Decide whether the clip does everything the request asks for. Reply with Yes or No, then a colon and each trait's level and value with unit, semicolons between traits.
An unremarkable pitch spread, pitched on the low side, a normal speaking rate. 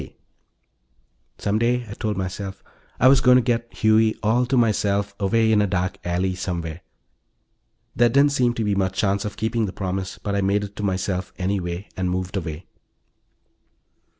Yes: average, 3.3 semitones; low, 100 Hz; average, 180 wpm